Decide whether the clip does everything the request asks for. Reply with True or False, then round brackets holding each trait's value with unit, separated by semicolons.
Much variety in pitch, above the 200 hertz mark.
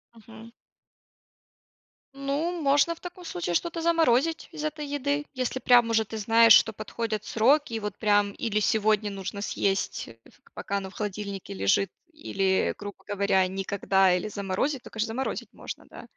True (5.7 semitones; 220 Hz)